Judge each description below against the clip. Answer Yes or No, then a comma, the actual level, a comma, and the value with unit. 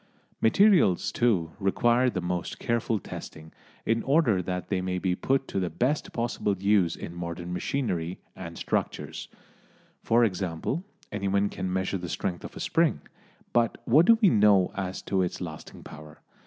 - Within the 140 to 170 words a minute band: Yes, average, 160 wpm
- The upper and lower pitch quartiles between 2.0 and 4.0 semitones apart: No, average, 4.8 semitones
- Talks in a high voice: No, very low, 95 Hz